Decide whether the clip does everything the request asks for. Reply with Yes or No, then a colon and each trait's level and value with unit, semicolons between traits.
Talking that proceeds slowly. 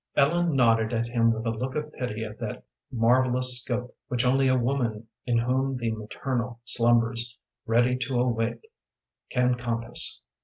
No: average, 155 wpm